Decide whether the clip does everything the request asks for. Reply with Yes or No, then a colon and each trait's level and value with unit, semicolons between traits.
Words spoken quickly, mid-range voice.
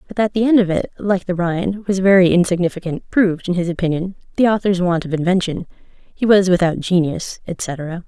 No: average, 195 wpm; medium, 180 Hz